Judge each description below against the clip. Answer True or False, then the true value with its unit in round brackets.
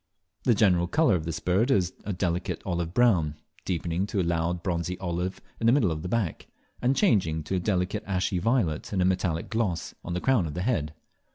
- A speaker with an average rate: False (215 wpm)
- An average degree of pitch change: True (3.6 semitones)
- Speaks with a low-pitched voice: True (90 Hz)